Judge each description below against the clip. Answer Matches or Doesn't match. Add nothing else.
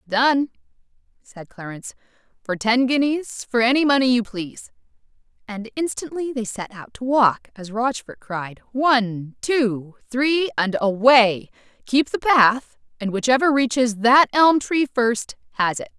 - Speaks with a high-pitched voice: Matches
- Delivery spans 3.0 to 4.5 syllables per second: Matches